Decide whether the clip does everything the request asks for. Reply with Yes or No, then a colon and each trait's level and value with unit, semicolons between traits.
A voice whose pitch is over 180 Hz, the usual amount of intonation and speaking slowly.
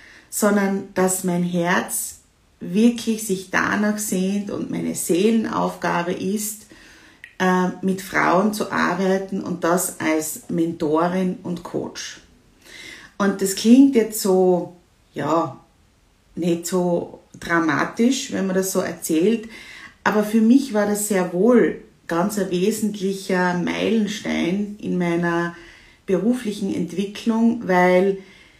Yes: high, 190 Hz; average, 3.1 semitones; slow, 110 wpm